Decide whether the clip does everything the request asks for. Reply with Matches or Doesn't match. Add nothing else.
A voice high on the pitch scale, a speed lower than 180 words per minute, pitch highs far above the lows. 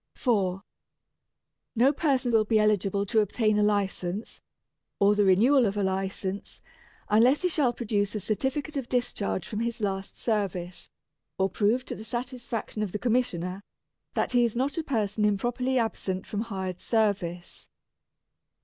Doesn't match